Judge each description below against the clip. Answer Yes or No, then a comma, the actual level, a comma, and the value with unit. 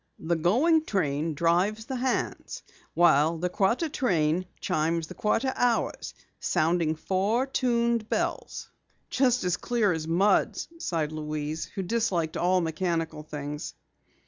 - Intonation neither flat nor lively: No, wide, 6.2 semitones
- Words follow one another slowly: Yes, slow, 125 wpm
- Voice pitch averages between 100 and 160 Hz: No, medium, 175 Hz